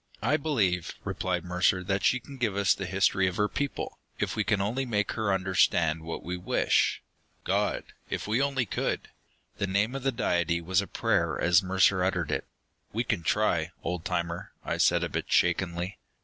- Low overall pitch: Yes, very low, 95 Hz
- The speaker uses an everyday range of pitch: Yes, average, 3.6 semitones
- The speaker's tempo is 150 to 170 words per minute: No, average, 190 wpm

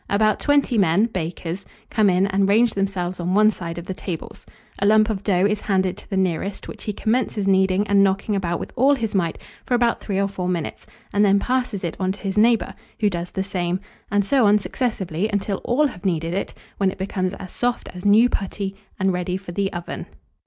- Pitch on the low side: No, high, 195 Hz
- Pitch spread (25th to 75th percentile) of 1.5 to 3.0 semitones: Yes, narrow, 2.4 semitones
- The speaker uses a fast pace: Yes, fast, 220 wpm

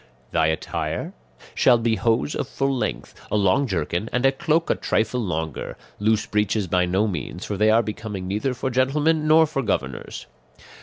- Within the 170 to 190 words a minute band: Yes, average, 175 wpm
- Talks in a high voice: No, low, 110 Hz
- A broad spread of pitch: Yes, wide, 5.8 semitones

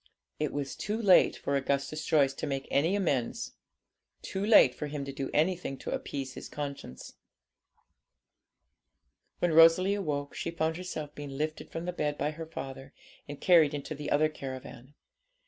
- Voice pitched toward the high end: No, medium, 150 Hz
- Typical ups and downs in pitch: Yes, average, 3.0 semitones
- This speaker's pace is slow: No, average, 165 wpm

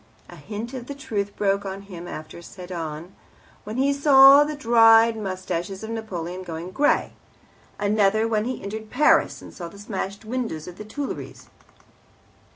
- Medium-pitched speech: No, high, 210 Hz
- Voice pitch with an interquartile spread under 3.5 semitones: No, average, 3.9 semitones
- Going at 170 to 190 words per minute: No, average, 160 wpm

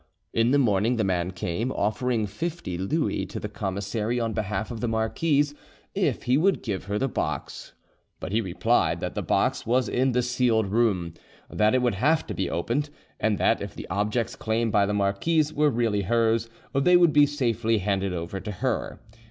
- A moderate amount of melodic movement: Yes, average, 4.0 semitones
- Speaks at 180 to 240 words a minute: Yes, average, 195 wpm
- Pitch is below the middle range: Yes, low, 115 Hz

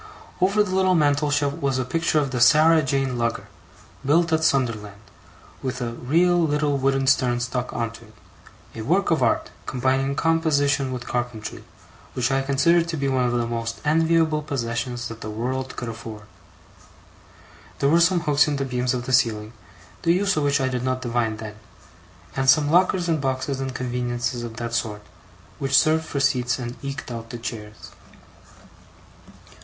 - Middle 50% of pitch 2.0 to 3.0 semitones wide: No, average, 3.8 semitones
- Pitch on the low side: Yes, low, 130 Hz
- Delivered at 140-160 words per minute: No, average, 175 wpm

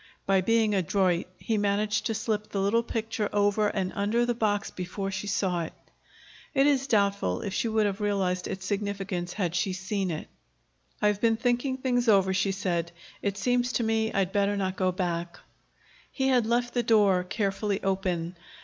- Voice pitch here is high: Yes, high, 200 Hz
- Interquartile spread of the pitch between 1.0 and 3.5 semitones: Yes, average, 2.9 semitones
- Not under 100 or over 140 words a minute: No, average, 180 wpm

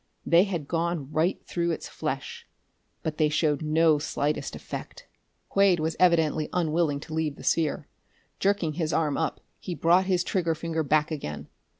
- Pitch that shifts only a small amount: Yes, narrow, 2.2 semitones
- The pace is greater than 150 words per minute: Yes, average, 165 wpm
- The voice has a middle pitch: Yes, medium, 160 Hz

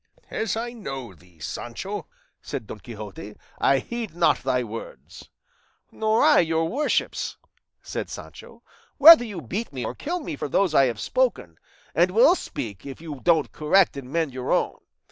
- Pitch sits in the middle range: Yes, medium, 165 Hz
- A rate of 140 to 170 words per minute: Yes, average, 165 wpm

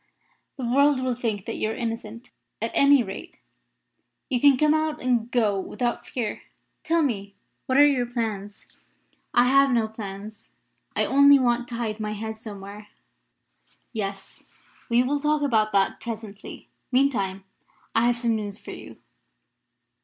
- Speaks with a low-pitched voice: No, high, 235 Hz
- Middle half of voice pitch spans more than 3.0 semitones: Yes, average, 3.5 semitones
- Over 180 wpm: No, average, 155 wpm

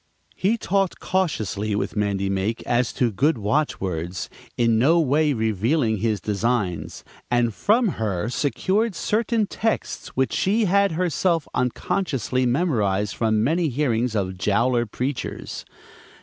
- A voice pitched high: No, low, 125 Hz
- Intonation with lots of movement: Yes, wide, 7.8 semitones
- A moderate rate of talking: No, slow, 130 wpm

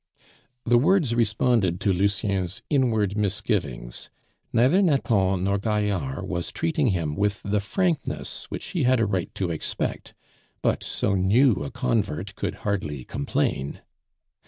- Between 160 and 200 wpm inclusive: No, slow, 135 wpm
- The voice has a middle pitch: No, low, 100 Hz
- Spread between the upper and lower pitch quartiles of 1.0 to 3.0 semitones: No, average, 4.6 semitones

